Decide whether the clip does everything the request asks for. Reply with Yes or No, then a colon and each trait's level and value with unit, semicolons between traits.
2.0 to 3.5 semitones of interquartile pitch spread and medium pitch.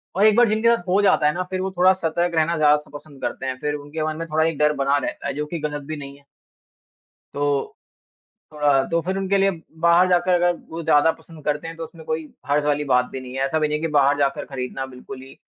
Yes: average, 3.0 semitones; medium, 155 Hz